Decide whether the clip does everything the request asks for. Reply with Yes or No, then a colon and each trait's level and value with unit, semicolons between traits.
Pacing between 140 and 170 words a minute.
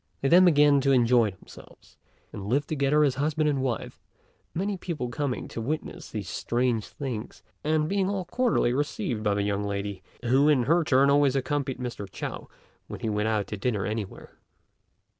No: average, 180 wpm